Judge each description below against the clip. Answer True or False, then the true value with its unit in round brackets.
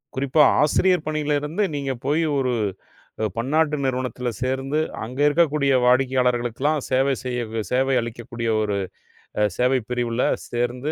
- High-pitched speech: False (130 Hz)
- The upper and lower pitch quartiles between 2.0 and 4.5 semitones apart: True (3.2 semitones)